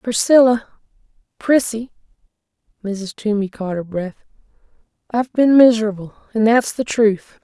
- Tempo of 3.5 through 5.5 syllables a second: Yes, 4.7 syllables/s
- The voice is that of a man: No, female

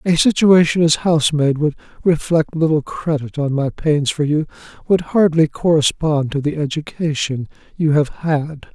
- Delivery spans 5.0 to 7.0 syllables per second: No, 4.6 syllables/s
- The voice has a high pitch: No, medium, 155 Hz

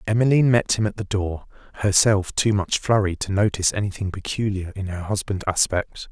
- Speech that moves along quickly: No, average, 175 wpm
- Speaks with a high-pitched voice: No, low, 100 Hz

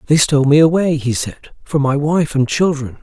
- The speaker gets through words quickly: Yes, fast, 220 wpm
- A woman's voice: No, male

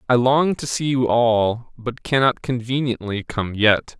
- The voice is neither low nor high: No, low, 120 Hz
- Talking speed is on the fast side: No, average, 165 wpm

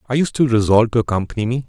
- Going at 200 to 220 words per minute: No, fast, 250 wpm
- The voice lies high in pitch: No, low, 120 Hz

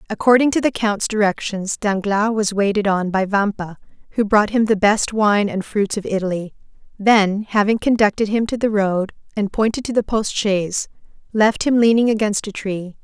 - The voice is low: No, high, 210 Hz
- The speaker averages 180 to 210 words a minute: Yes, average, 185 wpm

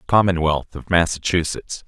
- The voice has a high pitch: No, very low, 85 Hz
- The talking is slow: Yes, slow, 95 wpm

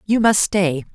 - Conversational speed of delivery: Yes, average, 190 wpm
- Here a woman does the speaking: Yes, female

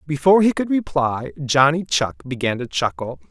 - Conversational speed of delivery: Yes, average, 165 wpm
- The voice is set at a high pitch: No, medium, 140 Hz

